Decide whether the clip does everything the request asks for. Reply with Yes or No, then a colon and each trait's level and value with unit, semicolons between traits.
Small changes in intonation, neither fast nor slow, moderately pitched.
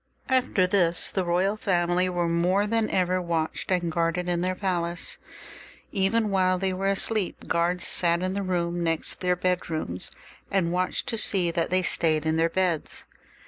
Yes: narrow, 1.8 semitones; average, 170 wpm; medium, 180 Hz